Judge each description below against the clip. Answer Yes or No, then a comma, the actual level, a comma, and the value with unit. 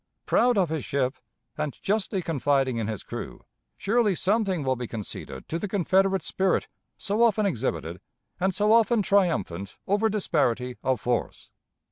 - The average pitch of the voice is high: No, medium, 180 Hz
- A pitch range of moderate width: No, wide, 8.1 semitones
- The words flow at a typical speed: Yes, average, 150 wpm